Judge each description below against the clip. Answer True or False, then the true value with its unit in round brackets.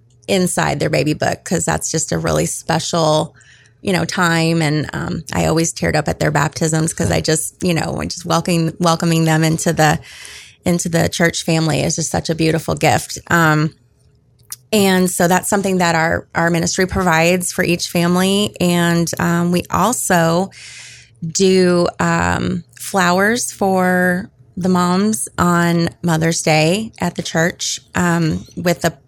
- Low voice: False (170 Hz)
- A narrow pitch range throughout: True (2.0 semitones)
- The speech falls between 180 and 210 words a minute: False (155 wpm)